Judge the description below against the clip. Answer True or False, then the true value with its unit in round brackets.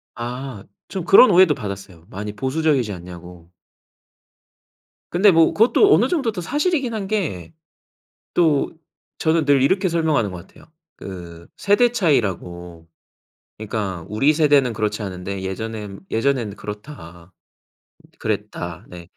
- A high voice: False (115 Hz)